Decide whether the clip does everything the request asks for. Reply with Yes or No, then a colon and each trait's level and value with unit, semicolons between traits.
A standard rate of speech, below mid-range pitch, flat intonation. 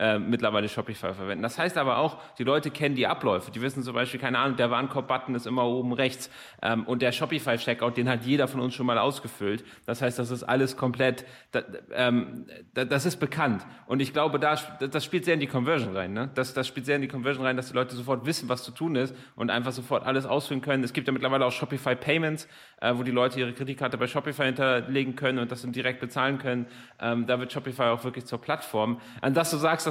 No: fast, 235 wpm; low, 130 Hz; narrow, 2.1 semitones